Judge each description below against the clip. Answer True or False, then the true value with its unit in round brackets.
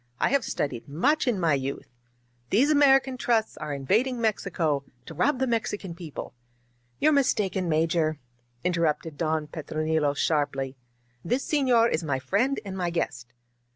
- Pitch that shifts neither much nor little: False (8.2 semitones)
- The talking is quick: False (155 wpm)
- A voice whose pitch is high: False (170 Hz)